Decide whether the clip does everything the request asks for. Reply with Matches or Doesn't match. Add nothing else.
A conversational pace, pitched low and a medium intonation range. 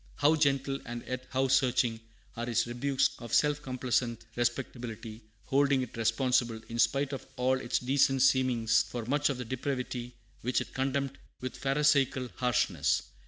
Doesn't match